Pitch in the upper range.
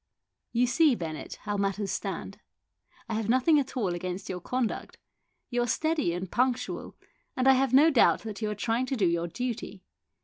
Yes: high, 230 Hz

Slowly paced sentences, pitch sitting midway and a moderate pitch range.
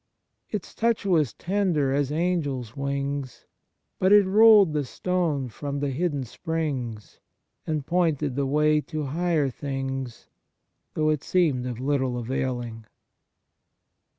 Yes: slow, 125 wpm; medium, 145 Hz; average, 4.2 semitones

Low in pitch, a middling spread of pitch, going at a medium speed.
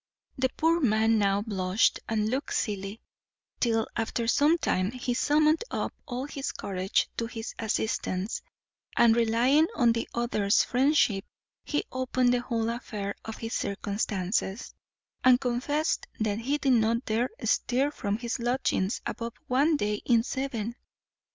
No: high, 235 Hz; average, 3.3 semitones; average, 145 wpm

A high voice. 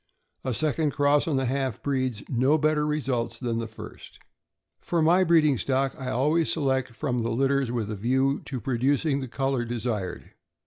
No: low, 135 Hz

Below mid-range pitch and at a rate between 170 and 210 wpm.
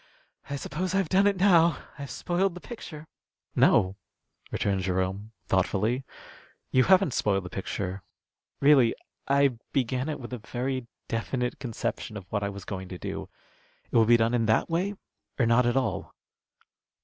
No: low, 125 Hz; average, 160 wpm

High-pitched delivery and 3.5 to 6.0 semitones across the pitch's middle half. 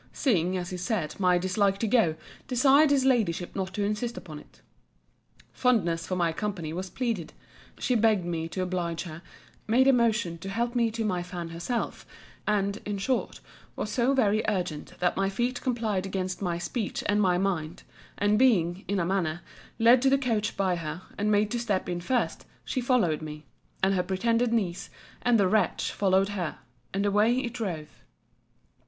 Yes: high, 195 Hz; average, 4.7 semitones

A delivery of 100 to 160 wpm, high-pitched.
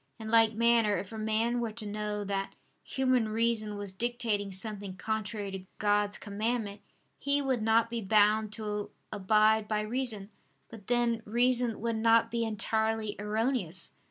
Yes: average, 155 wpm; high, 220 Hz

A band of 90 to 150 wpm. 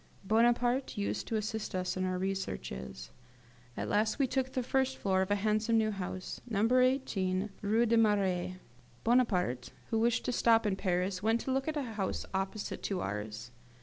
No: average, 180 wpm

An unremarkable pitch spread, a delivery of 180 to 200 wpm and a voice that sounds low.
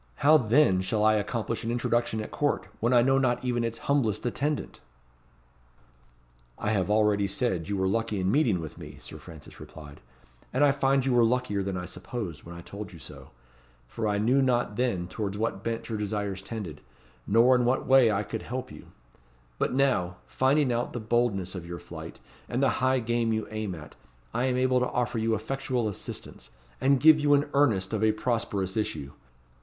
Yes: average, 4.0 semitones; average, 195 wpm; low, 115 Hz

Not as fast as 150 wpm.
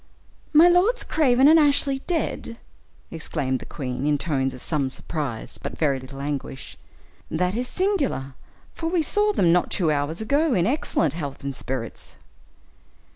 No: average, 155 wpm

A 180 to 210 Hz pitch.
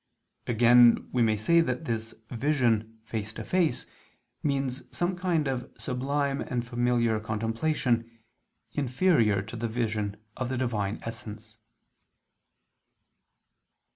No: low, 120 Hz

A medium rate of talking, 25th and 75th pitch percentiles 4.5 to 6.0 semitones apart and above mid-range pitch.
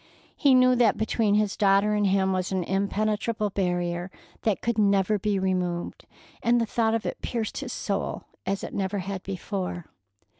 No: average, 175 wpm; narrow, 2.4 semitones; high, 200 Hz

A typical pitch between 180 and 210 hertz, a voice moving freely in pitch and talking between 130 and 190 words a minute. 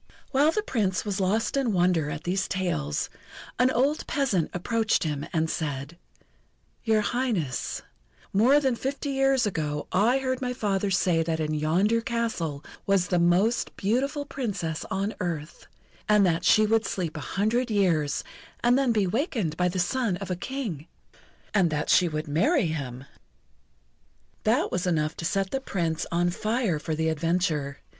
Yes: high, 190 Hz; wide, 6.3 semitones; average, 165 wpm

